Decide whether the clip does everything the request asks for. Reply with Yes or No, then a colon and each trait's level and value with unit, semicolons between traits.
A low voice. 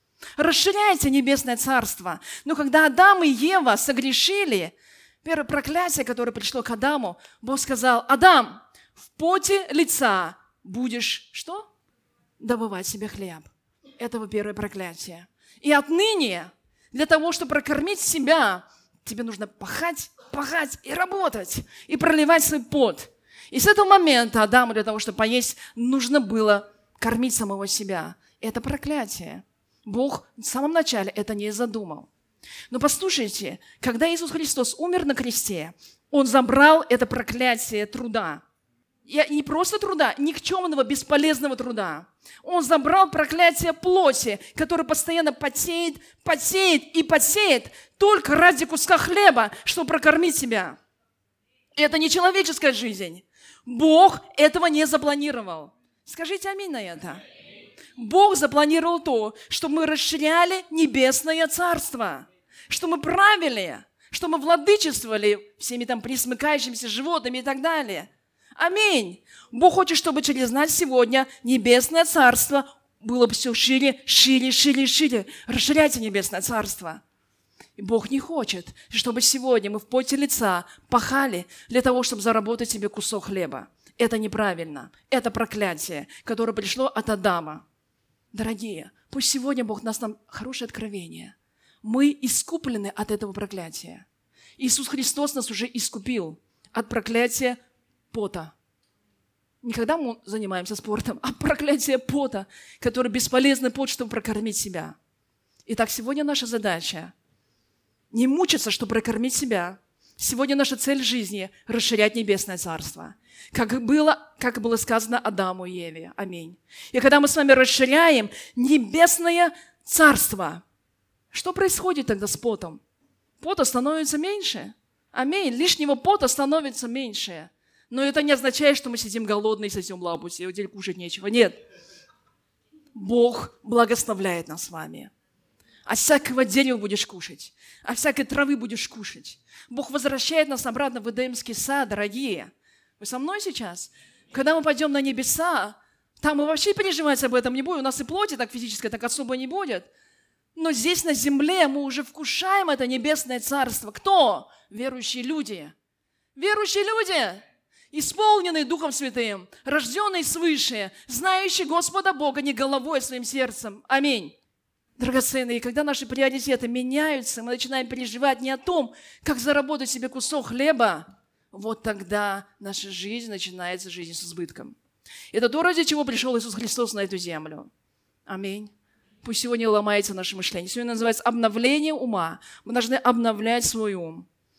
No: very high, 255 Hz